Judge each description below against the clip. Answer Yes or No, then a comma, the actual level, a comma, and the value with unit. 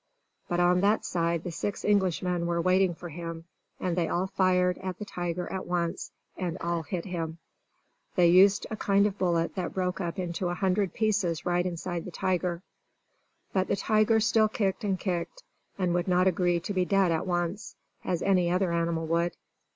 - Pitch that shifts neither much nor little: No, narrow, 1.8 semitones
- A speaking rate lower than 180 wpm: No, average, 190 wpm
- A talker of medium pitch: Yes, medium, 180 Hz